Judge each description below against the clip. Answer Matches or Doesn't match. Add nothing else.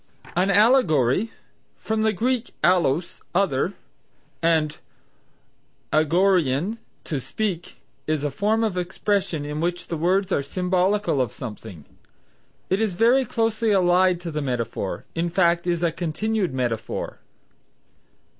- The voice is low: Doesn't match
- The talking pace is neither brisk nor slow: Doesn't match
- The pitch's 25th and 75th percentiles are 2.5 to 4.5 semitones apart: Doesn't match